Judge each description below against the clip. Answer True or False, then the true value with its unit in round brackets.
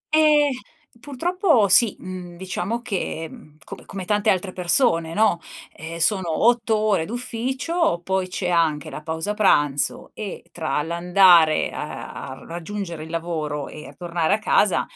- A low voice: False (185 Hz)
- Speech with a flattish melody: False (4.9 semitones)